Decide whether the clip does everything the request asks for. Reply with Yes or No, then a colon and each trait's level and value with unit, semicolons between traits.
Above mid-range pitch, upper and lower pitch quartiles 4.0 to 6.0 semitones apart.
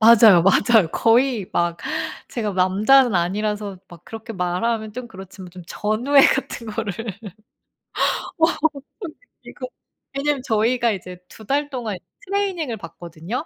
Yes: high, 220 Hz; average, 5.1 semitones